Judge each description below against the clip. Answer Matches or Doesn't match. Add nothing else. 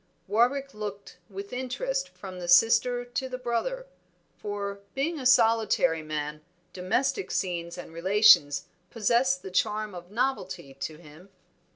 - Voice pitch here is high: Matches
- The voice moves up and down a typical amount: Doesn't match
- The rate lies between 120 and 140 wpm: Matches